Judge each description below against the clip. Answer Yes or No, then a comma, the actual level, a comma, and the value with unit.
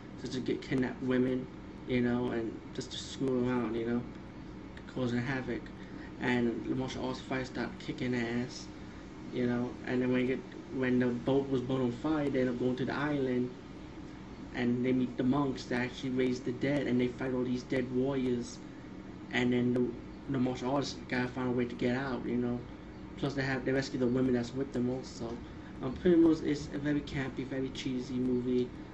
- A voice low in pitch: Yes, low, 125 Hz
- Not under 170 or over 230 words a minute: Yes, fast, 205 wpm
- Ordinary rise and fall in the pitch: No, narrow, 1.2 semitones